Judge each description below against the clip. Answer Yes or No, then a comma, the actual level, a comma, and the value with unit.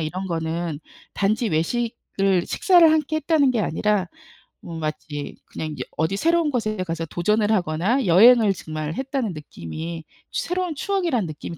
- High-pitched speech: Yes, high, 195 Hz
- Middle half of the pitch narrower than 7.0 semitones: No, wide, 8.0 semitones